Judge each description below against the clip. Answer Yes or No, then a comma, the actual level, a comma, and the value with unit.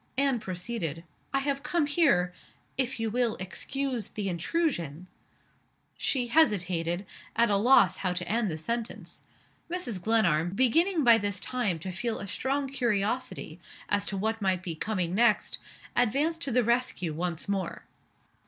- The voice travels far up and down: Yes, wide, 6.1 semitones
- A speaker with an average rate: Yes, average, 155 wpm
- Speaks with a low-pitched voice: No, high, 220 Hz